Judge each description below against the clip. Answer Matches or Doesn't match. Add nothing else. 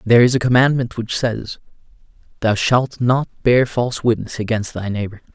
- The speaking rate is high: Doesn't match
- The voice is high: Doesn't match